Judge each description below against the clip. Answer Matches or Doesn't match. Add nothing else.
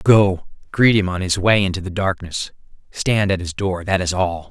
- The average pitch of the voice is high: Doesn't match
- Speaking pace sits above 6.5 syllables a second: Doesn't match